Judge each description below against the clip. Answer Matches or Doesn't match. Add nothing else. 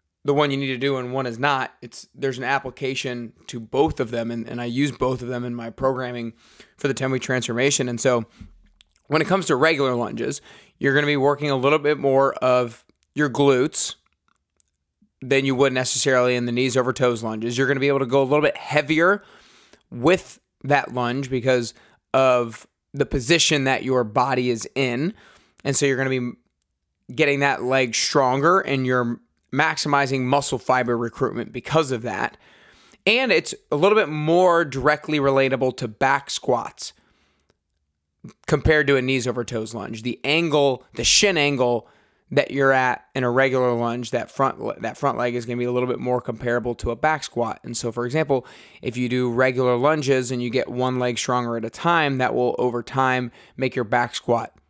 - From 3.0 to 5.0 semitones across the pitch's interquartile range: Doesn't match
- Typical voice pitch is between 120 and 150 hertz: Matches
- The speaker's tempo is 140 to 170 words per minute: Doesn't match